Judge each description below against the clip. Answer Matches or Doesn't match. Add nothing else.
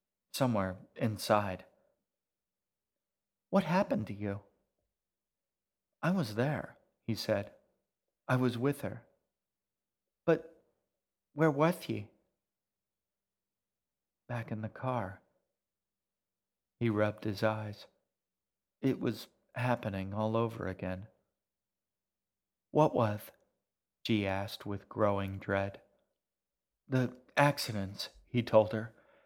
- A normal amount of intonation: Matches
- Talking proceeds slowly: Matches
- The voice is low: Matches